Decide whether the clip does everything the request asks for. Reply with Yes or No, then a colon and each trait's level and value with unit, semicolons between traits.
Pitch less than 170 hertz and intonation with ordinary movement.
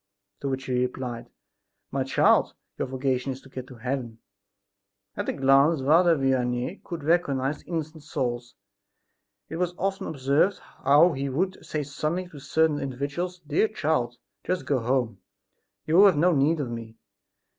Yes: medium, 140 Hz; average, 3.9 semitones